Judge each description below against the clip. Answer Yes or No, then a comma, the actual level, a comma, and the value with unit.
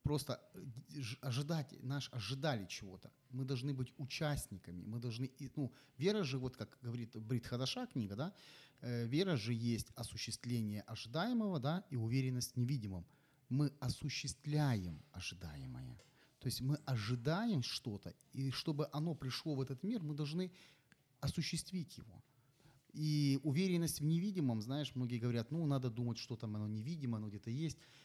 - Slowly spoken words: No, average, 145 wpm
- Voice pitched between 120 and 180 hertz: Yes, low, 135 Hz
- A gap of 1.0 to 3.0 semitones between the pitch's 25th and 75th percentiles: No, average, 3.8 semitones